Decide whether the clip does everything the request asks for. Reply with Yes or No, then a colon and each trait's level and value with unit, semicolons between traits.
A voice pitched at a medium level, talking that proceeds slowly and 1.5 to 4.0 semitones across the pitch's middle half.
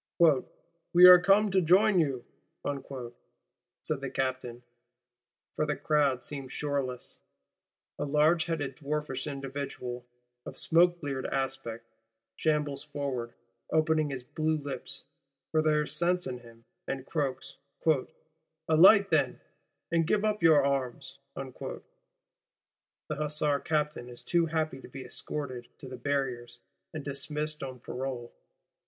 Yes: medium, 145 Hz; slow, 125 wpm; average, 3.2 semitones